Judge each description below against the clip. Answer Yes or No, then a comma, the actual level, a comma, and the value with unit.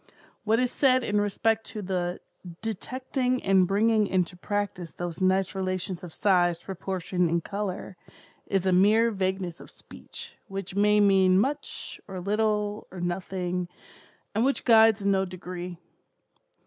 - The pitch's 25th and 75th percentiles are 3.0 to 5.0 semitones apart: No, narrow, 2.6 semitones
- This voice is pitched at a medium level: No, high, 195 Hz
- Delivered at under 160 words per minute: Yes, average, 145 wpm